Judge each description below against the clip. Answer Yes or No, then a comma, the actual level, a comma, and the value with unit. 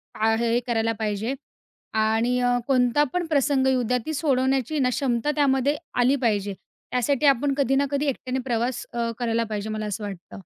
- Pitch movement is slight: No, average, 3.3 semitones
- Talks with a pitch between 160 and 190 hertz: No, very high, 250 Hz